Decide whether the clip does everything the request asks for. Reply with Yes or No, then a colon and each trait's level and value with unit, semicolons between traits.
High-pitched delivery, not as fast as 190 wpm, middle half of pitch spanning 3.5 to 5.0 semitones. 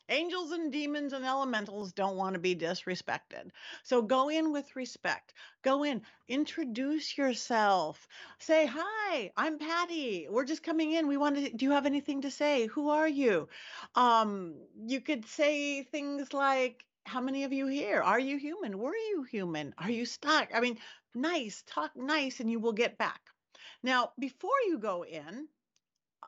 Yes: very high, 275 Hz; average, 170 wpm; average, 4.3 semitones